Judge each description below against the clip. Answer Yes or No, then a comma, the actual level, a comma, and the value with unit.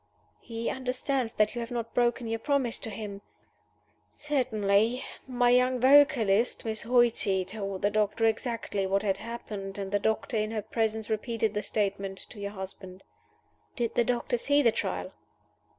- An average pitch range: Yes, average, 3.1 semitones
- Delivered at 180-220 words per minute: No, average, 160 wpm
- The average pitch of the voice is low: No, high, 225 Hz